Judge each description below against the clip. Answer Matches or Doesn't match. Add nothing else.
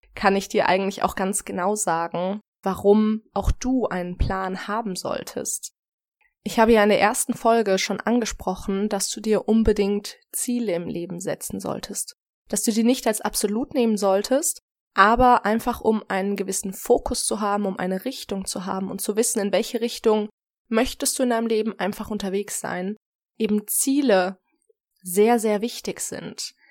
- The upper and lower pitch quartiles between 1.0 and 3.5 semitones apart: Matches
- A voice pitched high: Matches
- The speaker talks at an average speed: Matches